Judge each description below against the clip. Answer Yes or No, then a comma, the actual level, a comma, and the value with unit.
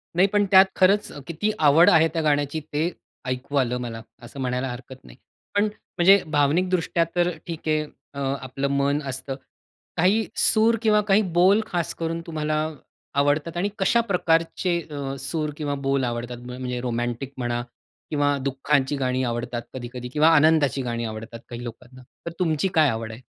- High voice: No, medium, 145 Hz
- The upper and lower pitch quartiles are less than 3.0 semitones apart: No, average, 4.9 semitones